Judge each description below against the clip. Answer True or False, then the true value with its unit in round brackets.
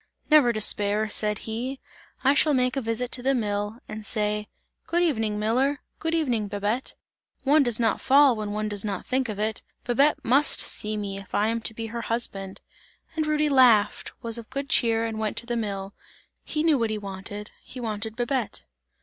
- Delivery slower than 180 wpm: False (195 wpm)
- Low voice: False (225 Hz)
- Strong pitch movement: False (3.8 semitones)